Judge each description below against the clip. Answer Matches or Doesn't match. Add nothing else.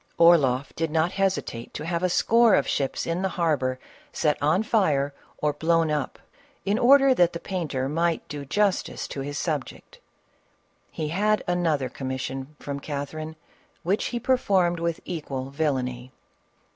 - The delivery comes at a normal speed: Matches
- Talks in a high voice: Doesn't match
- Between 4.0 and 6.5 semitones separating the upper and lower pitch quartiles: Matches